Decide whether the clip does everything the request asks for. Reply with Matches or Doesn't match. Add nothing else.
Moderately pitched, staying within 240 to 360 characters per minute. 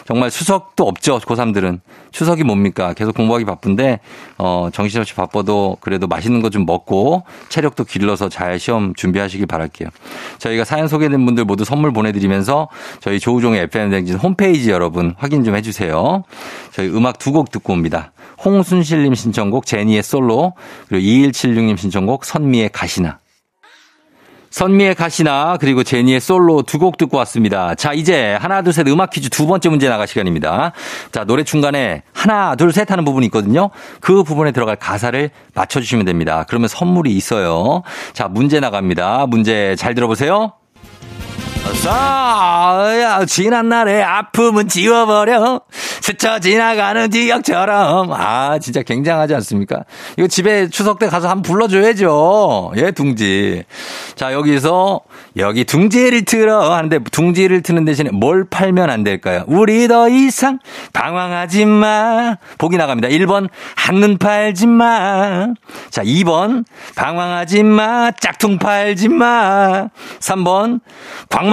Matches